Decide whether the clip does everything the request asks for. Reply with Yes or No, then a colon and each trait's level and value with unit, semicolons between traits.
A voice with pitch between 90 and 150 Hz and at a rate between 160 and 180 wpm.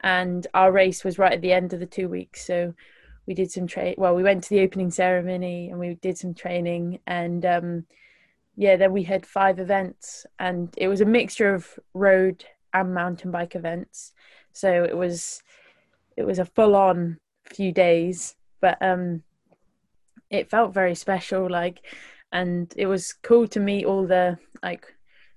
No: medium, 185 Hz; average, 175 wpm